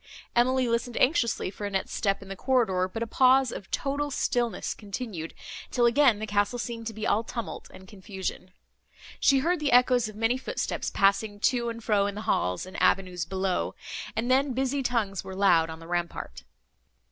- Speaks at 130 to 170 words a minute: No, average, 185 wpm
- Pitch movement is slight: No, average, 4.4 semitones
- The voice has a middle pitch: No, high, 225 Hz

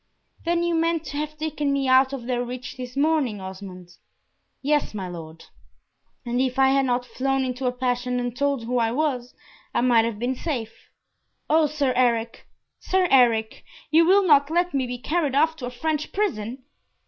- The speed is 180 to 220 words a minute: Yes, average, 185 wpm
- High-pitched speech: Yes, very high, 260 Hz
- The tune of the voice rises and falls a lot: No, average, 3.7 semitones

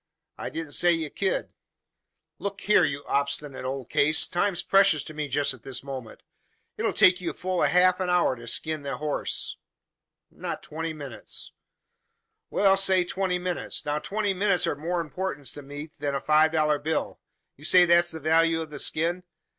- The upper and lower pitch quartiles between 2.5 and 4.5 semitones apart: Yes, average, 3.7 semitones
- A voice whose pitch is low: No, medium, 160 Hz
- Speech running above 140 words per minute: Yes, average, 185 wpm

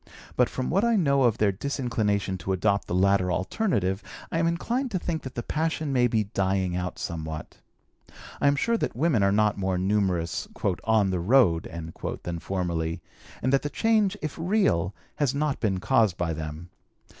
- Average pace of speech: Yes, average, 180 wpm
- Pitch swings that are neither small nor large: No, wide, 7.8 semitones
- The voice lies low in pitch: Yes, low, 105 Hz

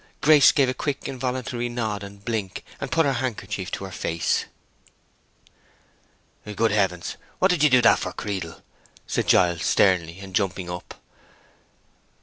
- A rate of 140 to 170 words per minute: Yes, average, 145 wpm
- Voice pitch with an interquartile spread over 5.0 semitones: Yes, wide, 5.5 semitones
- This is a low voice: Yes, low, 105 Hz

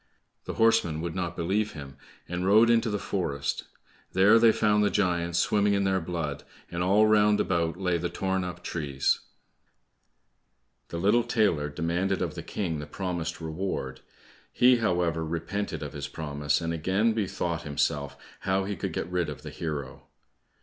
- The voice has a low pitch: Yes, very low, 90 Hz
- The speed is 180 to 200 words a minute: No, average, 165 wpm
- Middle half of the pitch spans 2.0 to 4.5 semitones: Yes, average, 4.0 semitones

